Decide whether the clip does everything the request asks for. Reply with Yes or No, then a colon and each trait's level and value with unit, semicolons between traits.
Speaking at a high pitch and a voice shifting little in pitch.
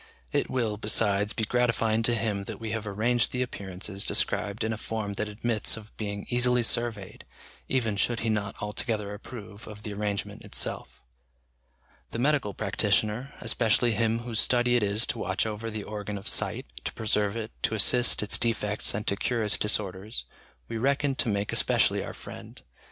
No: low, 110 Hz; narrow, 2.2 semitones